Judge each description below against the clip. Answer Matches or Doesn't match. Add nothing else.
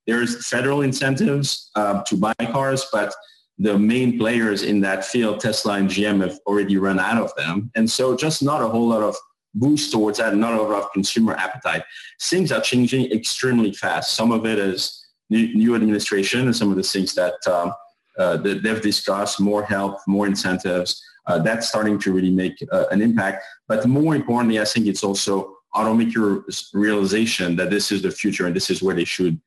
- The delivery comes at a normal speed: Matches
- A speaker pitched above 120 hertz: Doesn't match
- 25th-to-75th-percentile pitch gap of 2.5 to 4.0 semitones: Matches